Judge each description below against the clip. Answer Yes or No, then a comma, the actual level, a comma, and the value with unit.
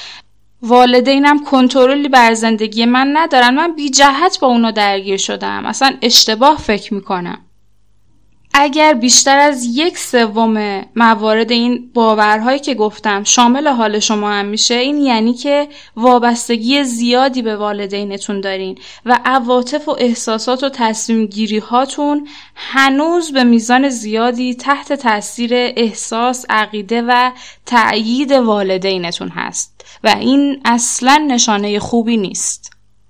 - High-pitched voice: Yes, high, 240 Hz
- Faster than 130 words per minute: No, average, 120 wpm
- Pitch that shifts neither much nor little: Yes, average, 3.9 semitones